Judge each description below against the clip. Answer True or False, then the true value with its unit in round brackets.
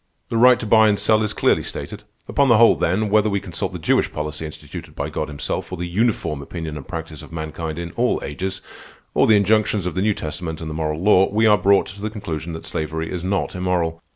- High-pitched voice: False (90 Hz)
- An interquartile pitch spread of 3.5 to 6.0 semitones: True (4.7 semitones)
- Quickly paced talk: True (235 wpm)